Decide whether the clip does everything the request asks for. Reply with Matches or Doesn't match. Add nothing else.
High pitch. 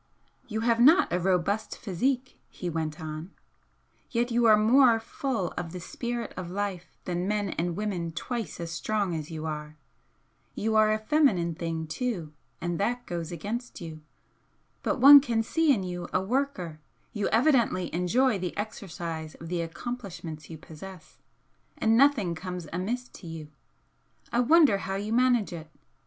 Matches